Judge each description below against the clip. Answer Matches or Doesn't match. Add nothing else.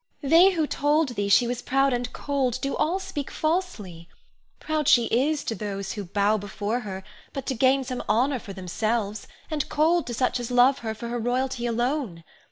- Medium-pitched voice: Doesn't match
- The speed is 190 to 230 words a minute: Matches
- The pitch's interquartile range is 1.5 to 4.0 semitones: Doesn't match